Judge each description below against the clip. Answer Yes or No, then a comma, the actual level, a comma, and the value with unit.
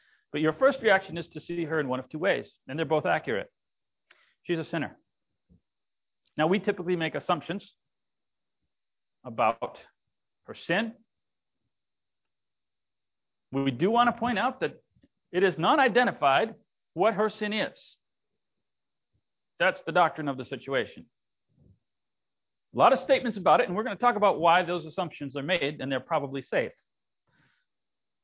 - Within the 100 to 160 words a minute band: Yes, average, 150 wpm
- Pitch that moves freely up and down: Yes, wide, 5.9 semitones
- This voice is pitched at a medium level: Yes, medium, 170 Hz